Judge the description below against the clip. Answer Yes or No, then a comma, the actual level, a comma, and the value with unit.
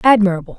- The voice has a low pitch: No, high, 205 Hz